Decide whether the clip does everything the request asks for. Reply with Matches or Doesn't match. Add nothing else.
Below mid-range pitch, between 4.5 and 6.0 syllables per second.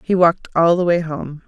Doesn't match